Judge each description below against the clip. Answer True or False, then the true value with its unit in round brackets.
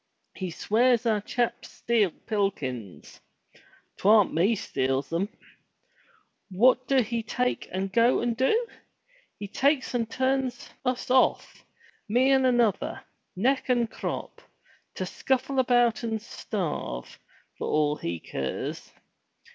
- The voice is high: True (230 Hz)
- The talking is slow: True (120 wpm)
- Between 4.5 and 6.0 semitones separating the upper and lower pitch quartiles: True (4.9 semitones)